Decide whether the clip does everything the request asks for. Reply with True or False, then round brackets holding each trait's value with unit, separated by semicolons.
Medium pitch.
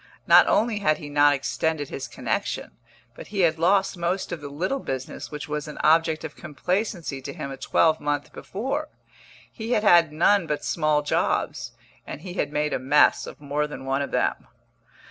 True (155 Hz)